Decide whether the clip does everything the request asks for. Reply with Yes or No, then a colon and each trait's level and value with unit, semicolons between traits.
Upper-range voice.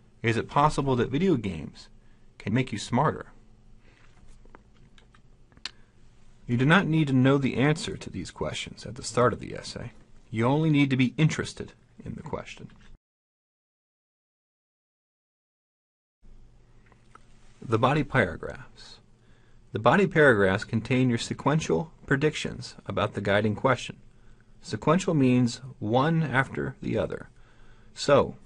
No: low, 120 Hz